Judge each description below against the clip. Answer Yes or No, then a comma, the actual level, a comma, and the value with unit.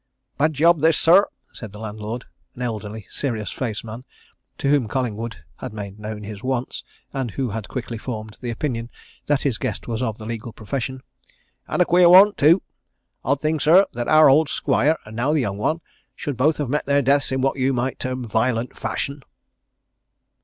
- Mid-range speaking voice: No, low, 130 Hz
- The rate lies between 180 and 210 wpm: Yes, average, 190 wpm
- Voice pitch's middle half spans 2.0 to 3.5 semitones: No, average, 4.5 semitones